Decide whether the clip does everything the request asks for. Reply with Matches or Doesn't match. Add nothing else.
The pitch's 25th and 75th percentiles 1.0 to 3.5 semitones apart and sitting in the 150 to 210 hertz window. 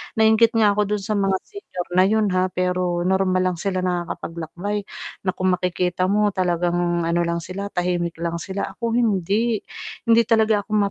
Matches